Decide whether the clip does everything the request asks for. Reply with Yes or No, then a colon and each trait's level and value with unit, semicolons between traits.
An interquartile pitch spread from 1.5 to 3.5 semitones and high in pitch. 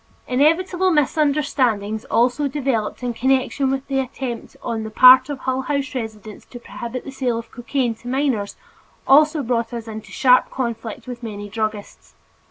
Yes: average, 3.2 semitones; very high, 250 Hz